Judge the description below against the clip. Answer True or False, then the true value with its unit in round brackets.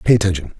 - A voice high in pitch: False (95 Hz)